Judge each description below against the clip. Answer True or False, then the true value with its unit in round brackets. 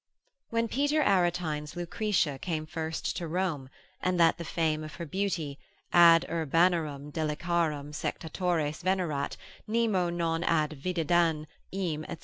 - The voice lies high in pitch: False (170 Hz)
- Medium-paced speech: False (130 wpm)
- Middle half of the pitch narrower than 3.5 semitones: True (2.8 semitones)